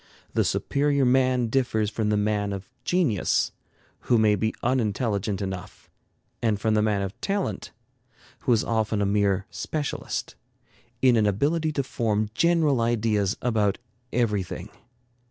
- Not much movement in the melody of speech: No, average, 3.7 semitones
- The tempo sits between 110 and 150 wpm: Yes, slow, 135 wpm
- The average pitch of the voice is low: Yes, low, 110 Hz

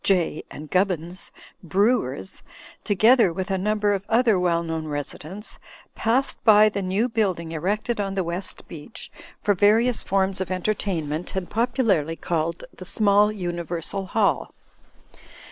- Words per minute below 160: Yes, average, 140 wpm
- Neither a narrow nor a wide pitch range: Yes, average, 3.8 semitones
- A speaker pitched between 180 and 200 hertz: Yes, high, 190 Hz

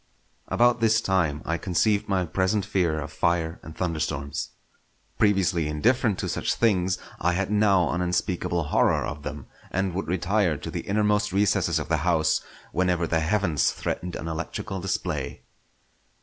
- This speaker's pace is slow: No, average, 155 wpm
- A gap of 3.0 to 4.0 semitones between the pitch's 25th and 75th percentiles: Yes, average, 3.6 semitones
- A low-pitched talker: Yes, very low, 90 Hz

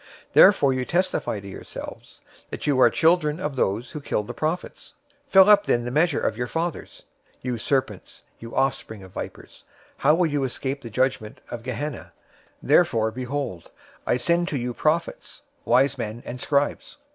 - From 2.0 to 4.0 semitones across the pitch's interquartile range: No, average, 4.4 semitones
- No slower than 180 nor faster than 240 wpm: Yes, average, 185 wpm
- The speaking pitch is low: Yes, low, 130 Hz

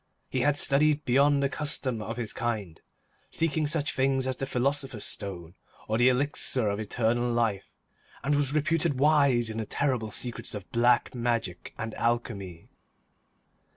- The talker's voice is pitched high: No, low, 125 Hz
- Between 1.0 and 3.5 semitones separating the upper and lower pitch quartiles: No, average, 4.1 semitones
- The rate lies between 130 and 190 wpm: Yes, average, 155 wpm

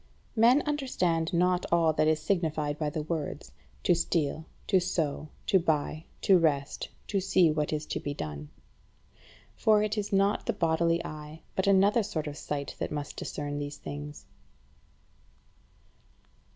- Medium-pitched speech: Yes, medium, 160 Hz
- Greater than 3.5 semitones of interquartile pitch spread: Yes, average, 4.2 semitones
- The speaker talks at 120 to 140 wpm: No, average, 155 wpm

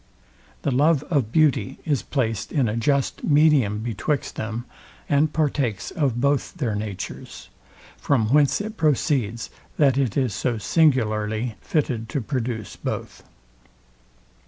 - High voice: No, low, 130 Hz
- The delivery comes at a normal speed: No, slow, 130 wpm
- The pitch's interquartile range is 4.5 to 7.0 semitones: Yes, average, 4.8 semitones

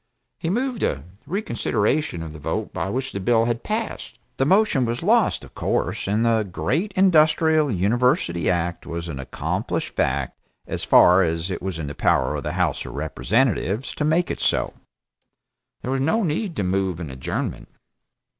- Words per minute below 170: No, average, 175 wpm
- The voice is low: Yes, low, 115 Hz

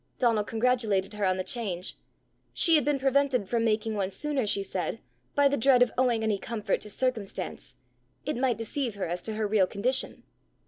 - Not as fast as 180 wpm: No, average, 190 wpm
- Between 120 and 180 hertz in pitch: No, high, 225 Hz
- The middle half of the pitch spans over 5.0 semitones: No, average, 4.2 semitones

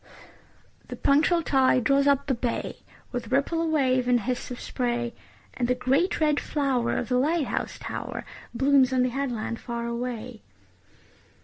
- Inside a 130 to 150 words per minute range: No, average, 165 wpm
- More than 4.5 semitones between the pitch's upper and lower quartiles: No, narrow, 2.5 semitones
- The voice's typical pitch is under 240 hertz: No, very high, 255 Hz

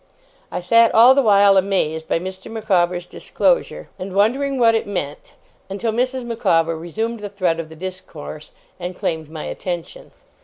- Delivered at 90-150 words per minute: No, average, 160 wpm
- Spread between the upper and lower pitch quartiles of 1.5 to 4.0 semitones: No, average, 4.9 semitones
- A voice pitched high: Yes, high, 195 Hz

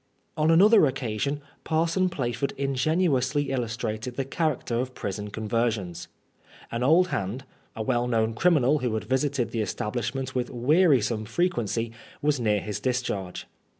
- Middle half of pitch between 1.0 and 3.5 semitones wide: No, average, 4.6 semitones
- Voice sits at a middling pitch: No, low, 125 Hz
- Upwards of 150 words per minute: No, slow, 135 wpm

